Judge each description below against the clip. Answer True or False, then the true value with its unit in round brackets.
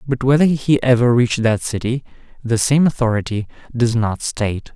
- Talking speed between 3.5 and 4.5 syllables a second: False (5.3 syllables/s)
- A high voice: False (120 Hz)